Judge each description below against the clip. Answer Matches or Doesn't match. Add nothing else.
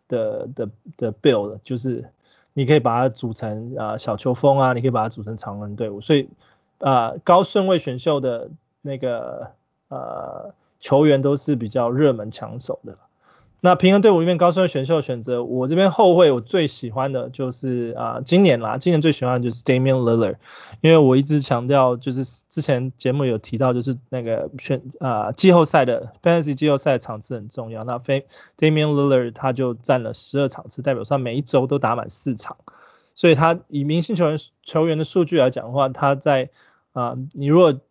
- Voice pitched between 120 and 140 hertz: Matches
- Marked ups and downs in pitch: Doesn't match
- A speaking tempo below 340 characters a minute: Matches